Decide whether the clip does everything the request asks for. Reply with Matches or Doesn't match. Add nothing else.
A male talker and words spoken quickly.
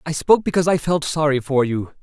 Matches